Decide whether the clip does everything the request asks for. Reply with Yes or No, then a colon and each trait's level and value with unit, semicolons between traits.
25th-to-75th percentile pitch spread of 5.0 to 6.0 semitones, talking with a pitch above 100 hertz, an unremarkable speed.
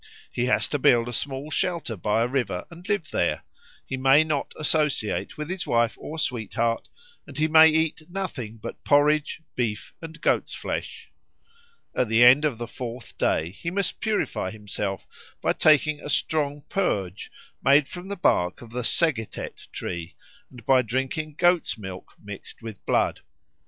Yes: wide, 5.6 semitones; low, 135 Hz; average, 165 wpm